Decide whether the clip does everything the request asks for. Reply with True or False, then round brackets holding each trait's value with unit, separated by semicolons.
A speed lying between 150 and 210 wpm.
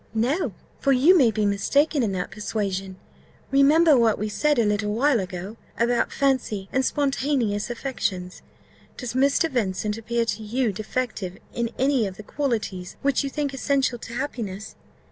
True (160 wpm)